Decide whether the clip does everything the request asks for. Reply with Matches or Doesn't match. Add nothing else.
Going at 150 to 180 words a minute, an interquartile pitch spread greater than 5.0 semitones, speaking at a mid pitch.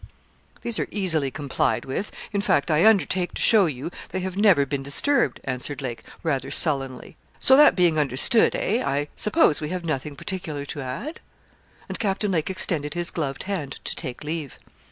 Matches